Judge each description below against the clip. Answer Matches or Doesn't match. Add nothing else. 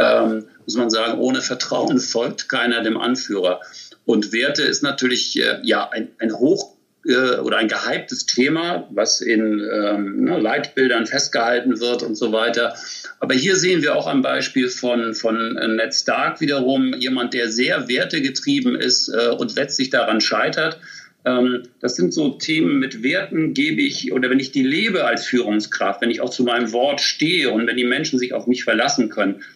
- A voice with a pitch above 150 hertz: Doesn't match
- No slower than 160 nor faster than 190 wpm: Matches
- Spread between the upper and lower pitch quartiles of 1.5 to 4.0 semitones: Matches